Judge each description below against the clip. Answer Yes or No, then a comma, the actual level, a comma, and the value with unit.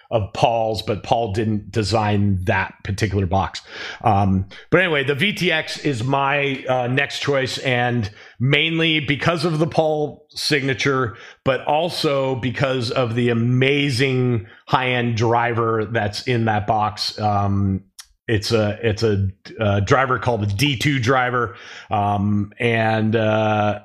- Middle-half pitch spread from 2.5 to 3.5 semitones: No, average, 4.6 semitones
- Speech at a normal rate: No, slow, 130 wpm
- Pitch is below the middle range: Yes, low, 120 Hz